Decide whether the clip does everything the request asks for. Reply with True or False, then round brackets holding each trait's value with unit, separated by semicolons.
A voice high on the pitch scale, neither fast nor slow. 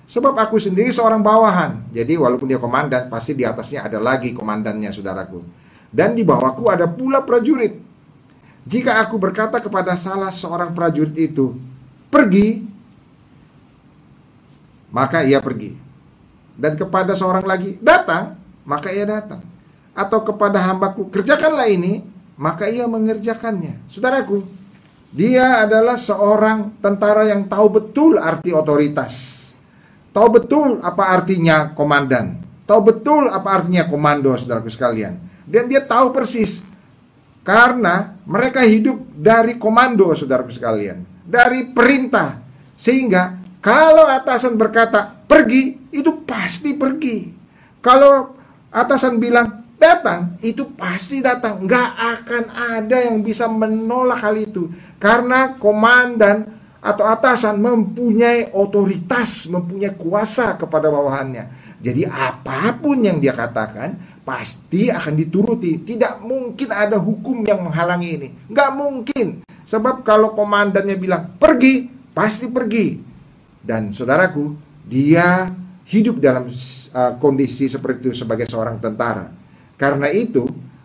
False (205 Hz; 115 wpm)